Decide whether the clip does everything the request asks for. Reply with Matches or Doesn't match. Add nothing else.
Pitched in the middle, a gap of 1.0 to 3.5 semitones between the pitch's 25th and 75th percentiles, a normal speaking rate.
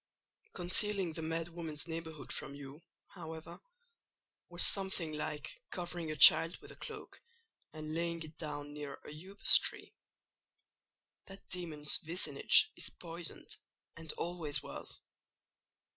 Doesn't match